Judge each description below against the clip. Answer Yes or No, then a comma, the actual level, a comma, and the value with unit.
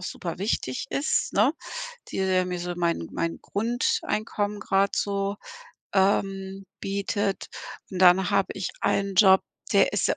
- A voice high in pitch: Yes, high, 195 Hz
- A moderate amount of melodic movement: No, narrow, 1.7 semitones